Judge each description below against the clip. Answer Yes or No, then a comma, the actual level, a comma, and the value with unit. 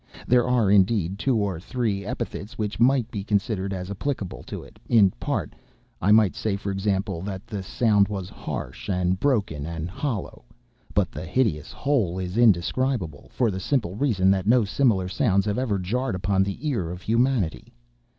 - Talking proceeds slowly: No, average, 175 wpm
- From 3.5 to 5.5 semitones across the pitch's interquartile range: Yes, average, 4.0 semitones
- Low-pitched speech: Yes, low, 100 Hz